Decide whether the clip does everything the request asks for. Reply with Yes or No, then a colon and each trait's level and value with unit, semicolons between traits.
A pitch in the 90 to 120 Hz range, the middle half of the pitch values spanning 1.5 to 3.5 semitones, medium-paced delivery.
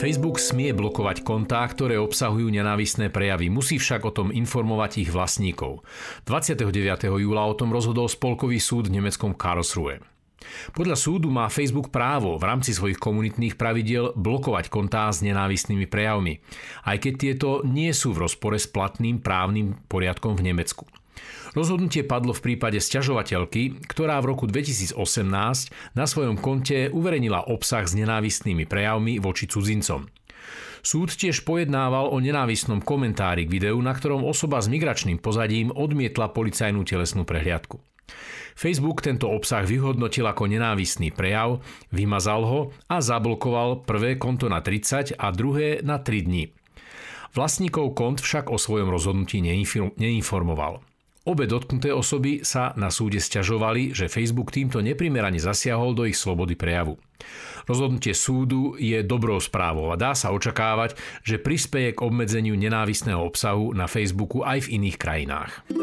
No: low, 115 Hz; average, 4.6 semitones; average, 140 wpm